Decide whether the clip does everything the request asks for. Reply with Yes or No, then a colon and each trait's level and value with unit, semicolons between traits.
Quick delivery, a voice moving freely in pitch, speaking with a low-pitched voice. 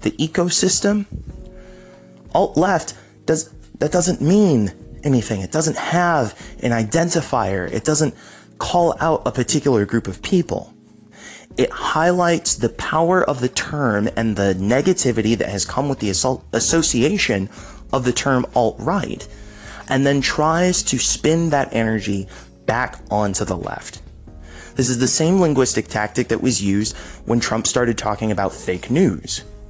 No: average, 145 wpm; wide, 7.1 semitones; low, 125 Hz